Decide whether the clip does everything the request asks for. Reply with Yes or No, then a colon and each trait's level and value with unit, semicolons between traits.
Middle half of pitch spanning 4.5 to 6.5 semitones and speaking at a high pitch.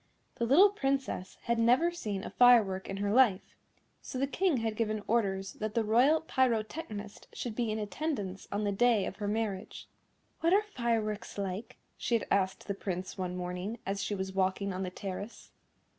No: average, 3.9 semitones; high, 215 Hz